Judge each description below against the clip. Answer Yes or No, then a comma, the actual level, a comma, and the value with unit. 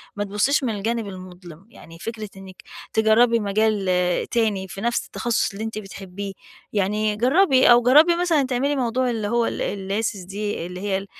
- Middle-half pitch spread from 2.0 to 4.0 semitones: Yes, average, 3.4 semitones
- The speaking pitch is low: No, high, 215 Hz